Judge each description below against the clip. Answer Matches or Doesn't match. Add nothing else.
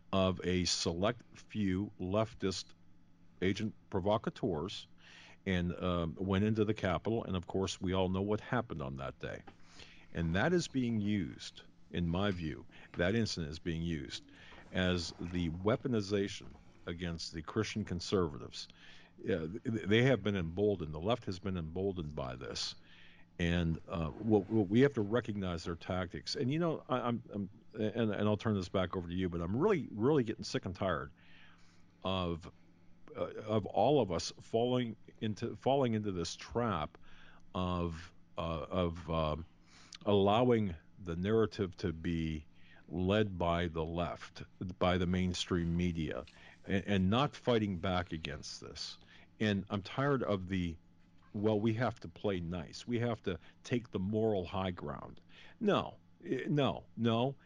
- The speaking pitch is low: Matches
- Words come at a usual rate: Matches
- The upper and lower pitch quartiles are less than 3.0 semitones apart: Doesn't match